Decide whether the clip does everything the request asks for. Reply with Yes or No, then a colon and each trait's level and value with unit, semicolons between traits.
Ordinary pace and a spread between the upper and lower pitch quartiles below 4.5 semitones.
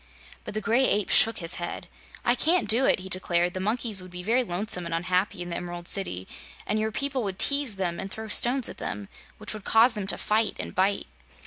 No: fast, 230 wpm; average, 4.0 semitones